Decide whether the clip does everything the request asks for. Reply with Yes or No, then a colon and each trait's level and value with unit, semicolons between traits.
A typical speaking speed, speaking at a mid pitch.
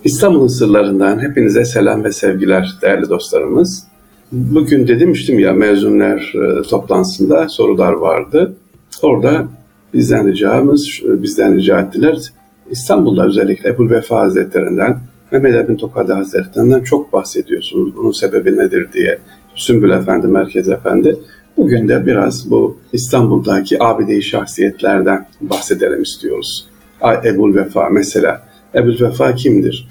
Yes: average, 110 wpm; medium, 145 Hz